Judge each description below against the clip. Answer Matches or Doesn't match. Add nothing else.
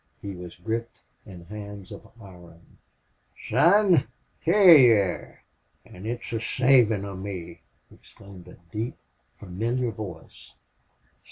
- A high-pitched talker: Doesn't match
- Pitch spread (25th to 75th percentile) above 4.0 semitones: Matches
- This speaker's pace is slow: Matches